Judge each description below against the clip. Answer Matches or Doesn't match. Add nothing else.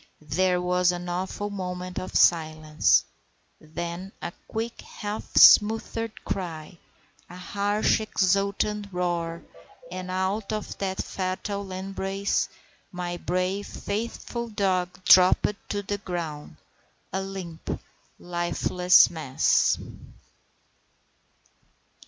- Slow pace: Matches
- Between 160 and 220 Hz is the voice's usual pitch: Matches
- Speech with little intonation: Matches